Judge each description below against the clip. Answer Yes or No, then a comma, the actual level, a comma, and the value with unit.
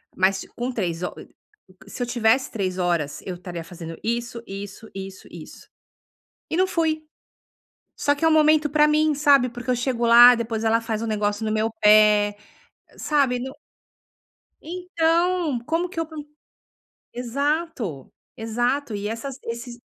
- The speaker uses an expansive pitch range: Yes, wide, 6.0 semitones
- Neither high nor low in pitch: No, high, 240 Hz